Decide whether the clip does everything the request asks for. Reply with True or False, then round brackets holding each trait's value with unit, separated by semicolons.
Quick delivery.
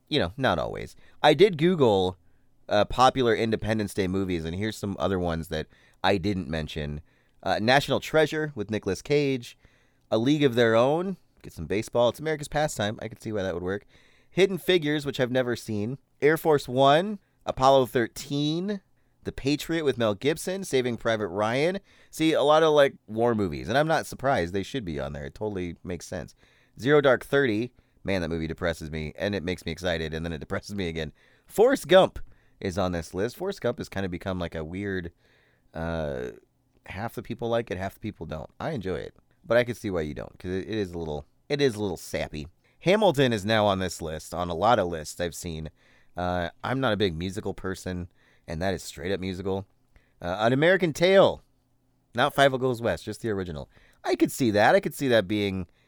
True (210 wpm)